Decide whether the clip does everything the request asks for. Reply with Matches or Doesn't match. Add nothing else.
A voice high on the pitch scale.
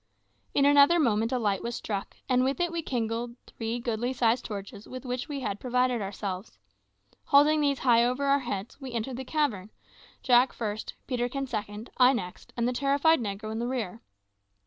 Matches